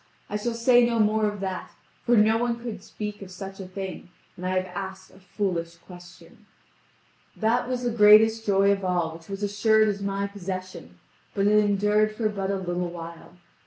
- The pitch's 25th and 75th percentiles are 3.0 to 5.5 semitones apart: No, narrow, 2.5 semitones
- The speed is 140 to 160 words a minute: No, average, 195 wpm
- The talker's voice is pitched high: Yes, high, 200 Hz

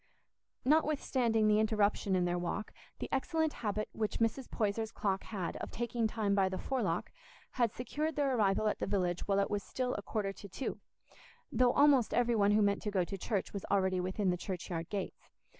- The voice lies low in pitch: No, high, 210 Hz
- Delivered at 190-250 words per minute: Yes, average, 195 wpm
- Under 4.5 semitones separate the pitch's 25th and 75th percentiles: Yes, average, 3.5 semitones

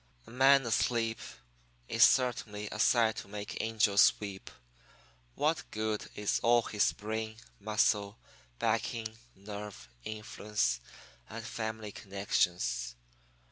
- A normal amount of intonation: No, narrow, 1.9 semitones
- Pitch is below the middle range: Yes, low, 110 Hz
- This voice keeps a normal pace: No, slow, 105 wpm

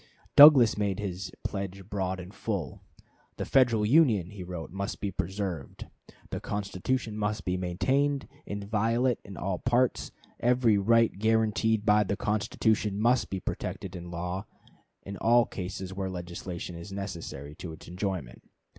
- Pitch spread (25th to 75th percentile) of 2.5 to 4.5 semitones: Yes, average, 3.4 semitones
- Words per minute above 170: No, average, 145 wpm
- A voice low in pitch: Yes, low, 100 Hz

